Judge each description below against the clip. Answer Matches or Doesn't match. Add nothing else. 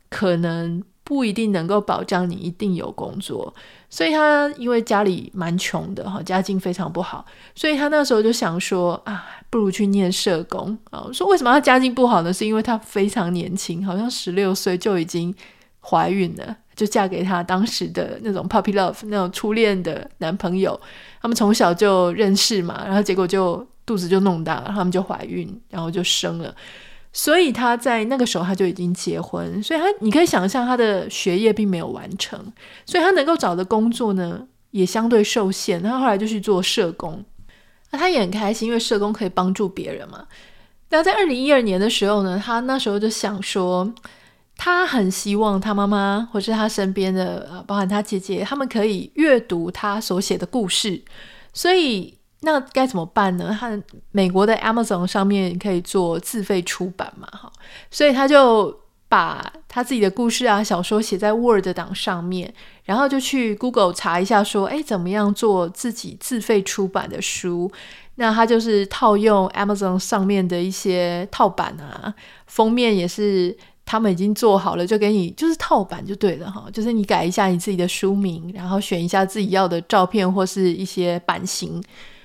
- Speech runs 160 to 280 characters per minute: Doesn't match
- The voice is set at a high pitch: Matches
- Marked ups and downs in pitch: Doesn't match